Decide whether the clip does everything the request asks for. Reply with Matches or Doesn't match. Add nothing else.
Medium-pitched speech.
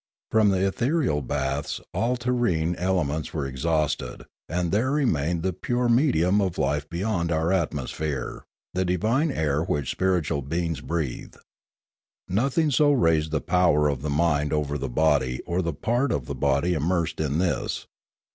Doesn't match